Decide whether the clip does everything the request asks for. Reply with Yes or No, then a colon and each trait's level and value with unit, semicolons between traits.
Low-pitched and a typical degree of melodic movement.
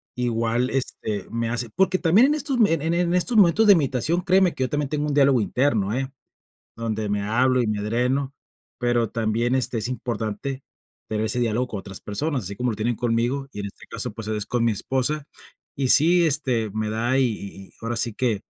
Yes: low, 125 Hz; average, 4.2 semitones